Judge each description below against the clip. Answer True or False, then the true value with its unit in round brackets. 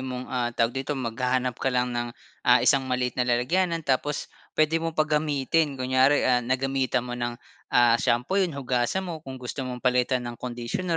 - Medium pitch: False (130 Hz)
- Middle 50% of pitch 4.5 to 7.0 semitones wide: False (3.0 semitones)